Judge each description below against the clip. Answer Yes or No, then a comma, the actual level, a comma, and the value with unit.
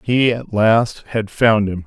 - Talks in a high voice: No, low, 110 Hz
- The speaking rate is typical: Yes, average, 195 wpm